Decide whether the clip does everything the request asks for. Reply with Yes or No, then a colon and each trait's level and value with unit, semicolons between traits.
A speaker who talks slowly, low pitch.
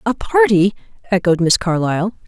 No: slow, 130 wpm; high, 200 Hz